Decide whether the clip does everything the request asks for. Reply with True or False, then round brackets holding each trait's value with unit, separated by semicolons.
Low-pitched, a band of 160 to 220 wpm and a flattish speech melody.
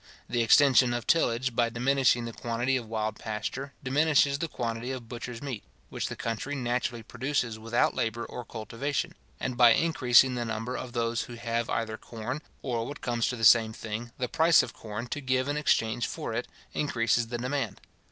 True (120 Hz; 190 wpm; 2.3 semitones)